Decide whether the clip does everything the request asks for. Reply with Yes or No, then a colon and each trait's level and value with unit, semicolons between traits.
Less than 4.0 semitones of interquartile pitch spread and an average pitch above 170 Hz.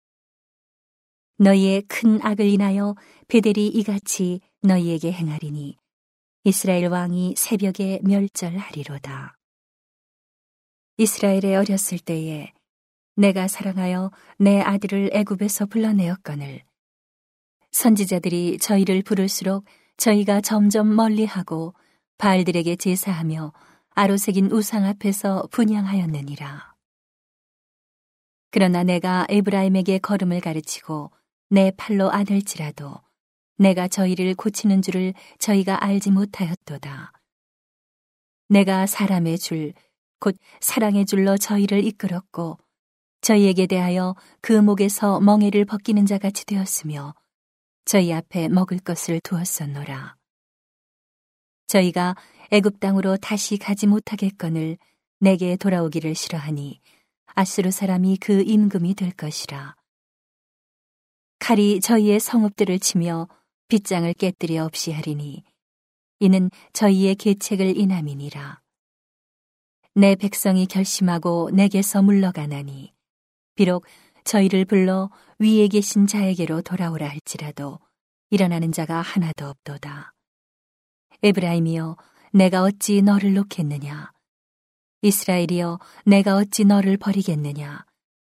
Yes: average, 2.8 semitones; high, 190 Hz